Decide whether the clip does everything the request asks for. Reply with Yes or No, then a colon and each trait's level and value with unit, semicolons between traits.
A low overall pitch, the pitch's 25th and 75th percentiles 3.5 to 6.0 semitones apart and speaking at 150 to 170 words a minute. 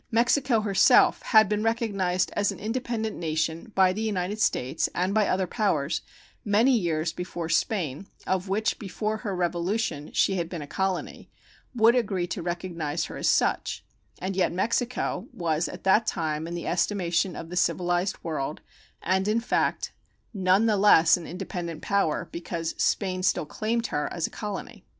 No: medium, 185 Hz; average, 3.9 semitones; average, 165 wpm